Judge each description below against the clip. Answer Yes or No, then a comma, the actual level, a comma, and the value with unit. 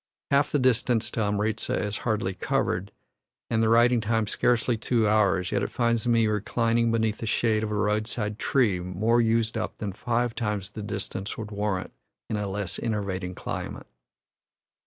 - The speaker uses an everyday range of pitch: No, narrow, 2.1 semitones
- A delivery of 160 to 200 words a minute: Yes, average, 170 wpm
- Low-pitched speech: Yes, low, 110 Hz